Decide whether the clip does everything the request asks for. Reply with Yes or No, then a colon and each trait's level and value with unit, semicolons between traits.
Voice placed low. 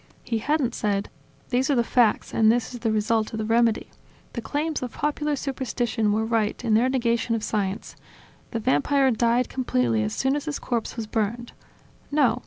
No: high, 235 Hz